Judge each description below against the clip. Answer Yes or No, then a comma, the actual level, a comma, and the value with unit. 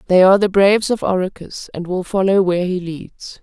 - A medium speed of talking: No, fast, 210 wpm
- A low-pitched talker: No, medium, 185 Hz